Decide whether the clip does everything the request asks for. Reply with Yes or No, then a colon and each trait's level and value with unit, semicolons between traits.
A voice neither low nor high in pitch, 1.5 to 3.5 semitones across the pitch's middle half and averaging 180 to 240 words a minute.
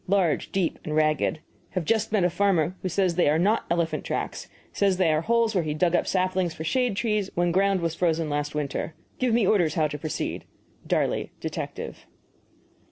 No: medium, 175 Hz; average, 3.9 semitones; average, 195 wpm